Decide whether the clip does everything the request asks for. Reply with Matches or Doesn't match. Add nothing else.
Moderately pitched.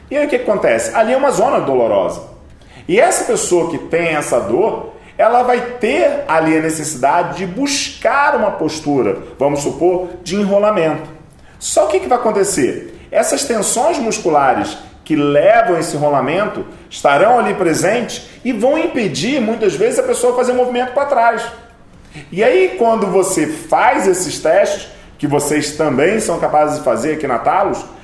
Doesn't match